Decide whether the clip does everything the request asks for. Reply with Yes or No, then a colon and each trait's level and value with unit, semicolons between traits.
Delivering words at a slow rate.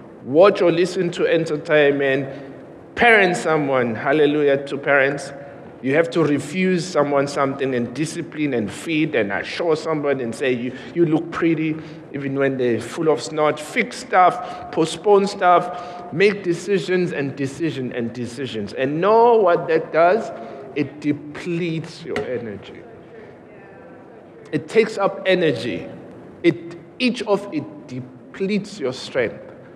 Yes: slow, 130 wpm